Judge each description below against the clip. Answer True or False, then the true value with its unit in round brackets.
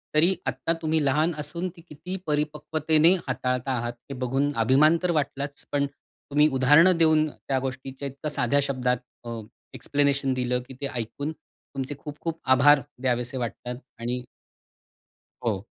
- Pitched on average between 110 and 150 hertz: True (140 Hz)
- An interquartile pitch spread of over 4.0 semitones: False (3.2 semitones)